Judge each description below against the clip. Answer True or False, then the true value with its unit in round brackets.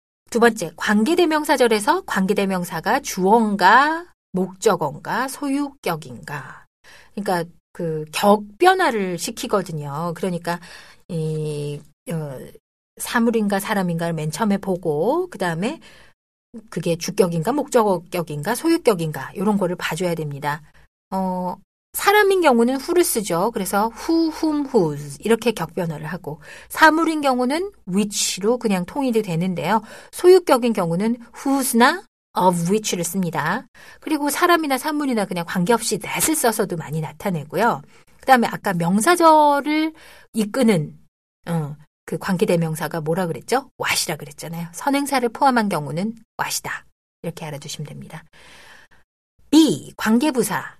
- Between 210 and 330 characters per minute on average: True (325 characters per minute)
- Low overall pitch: False (205 Hz)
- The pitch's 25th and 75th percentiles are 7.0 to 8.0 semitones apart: True (7.6 semitones)